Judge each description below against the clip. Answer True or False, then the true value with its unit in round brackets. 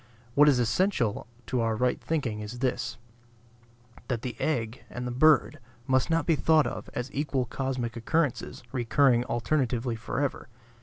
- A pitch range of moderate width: True (3.4 semitones)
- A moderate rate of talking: True (150 wpm)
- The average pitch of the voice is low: True (125 Hz)